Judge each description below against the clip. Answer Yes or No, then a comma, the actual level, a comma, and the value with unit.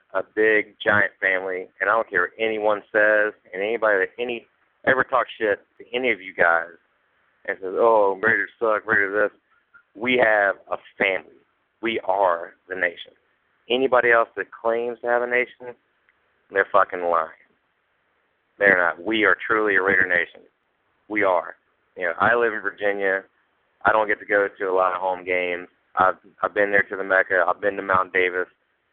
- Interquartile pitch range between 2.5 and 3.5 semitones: No, average, 4.3 semitones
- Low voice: Yes, low, 105 Hz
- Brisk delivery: No, average, 185 wpm